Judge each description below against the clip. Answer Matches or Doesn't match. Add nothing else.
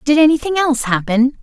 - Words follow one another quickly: Doesn't match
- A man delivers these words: Doesn't match